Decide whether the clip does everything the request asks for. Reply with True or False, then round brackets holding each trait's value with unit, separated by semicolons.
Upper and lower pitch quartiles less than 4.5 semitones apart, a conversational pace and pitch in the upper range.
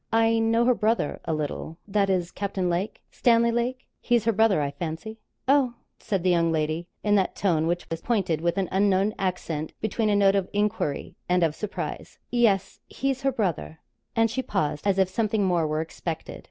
False (4.9 semitones; 195 wpm; 195 Hz)